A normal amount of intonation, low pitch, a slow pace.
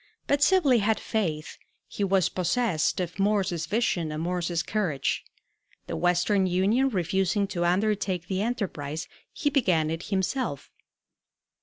No: average, 3.9 semitones; high, 190 Hz; slow, 130 wpm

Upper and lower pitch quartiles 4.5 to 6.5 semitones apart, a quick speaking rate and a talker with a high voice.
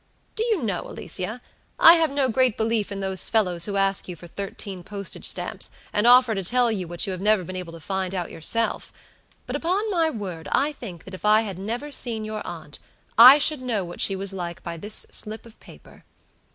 Yes: average, 4.8 semitones; fast, 220 wpm; high, 205 Hz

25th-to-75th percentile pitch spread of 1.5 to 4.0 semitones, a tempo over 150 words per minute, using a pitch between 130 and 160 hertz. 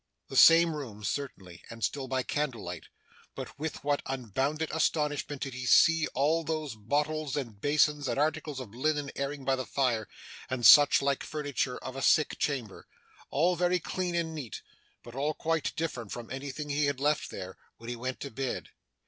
Yes: average, 3.2 semitones; average, 180 wpm; medium, 140 Hz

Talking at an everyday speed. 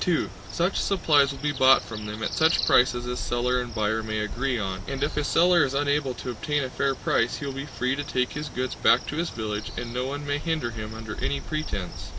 No: fast, 245 wpm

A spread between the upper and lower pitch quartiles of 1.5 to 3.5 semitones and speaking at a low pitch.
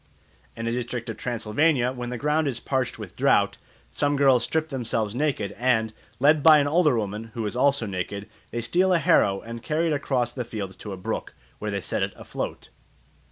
No: average, 4.4 semitones; low, 125 Hz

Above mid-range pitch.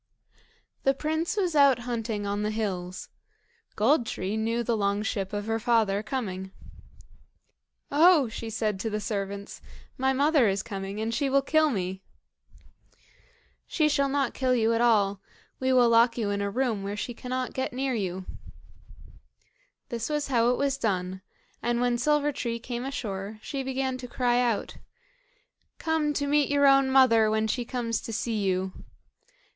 Yes: high, 235 Hz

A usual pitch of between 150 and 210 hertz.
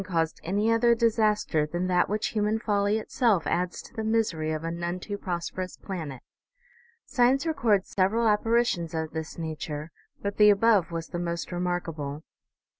Yes: medium, 185 Hz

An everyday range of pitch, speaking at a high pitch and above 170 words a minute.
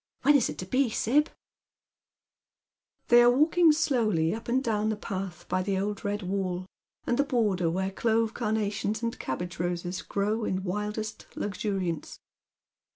No: average, 3.9 semitones; high, 210 Hz; average, 155 wpm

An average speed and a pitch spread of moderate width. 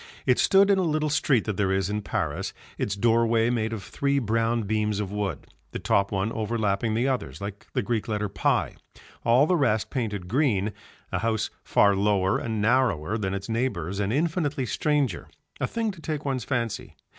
Yes: average, 190 wpm; average, 4.5 semitones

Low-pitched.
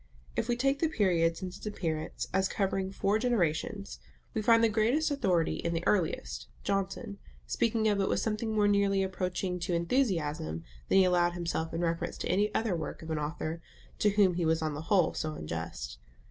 No: medium, 185 Hz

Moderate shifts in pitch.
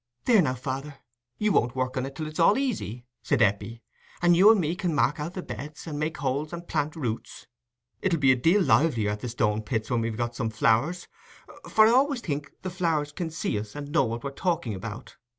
No: wide, 6.4 semitones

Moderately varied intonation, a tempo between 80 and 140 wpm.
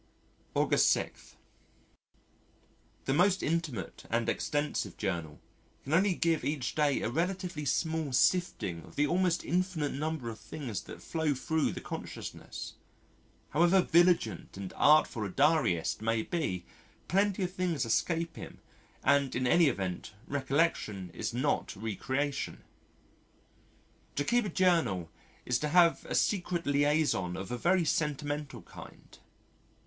No: wide, 6.1 semitones; slow, 135 wpm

